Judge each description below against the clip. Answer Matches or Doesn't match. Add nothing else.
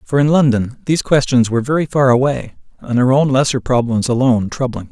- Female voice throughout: Doesn't match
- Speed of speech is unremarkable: Matches